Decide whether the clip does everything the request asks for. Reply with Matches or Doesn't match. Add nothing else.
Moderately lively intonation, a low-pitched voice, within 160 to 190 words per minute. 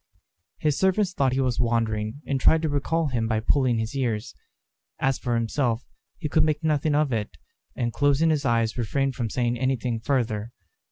Matches